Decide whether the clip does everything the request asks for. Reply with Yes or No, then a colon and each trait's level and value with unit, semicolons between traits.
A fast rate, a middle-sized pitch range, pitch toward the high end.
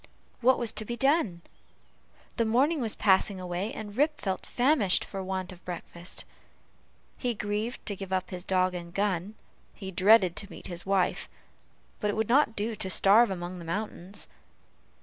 No: average, 175 wpm; average, 3.5 semitones; high, 200 Hz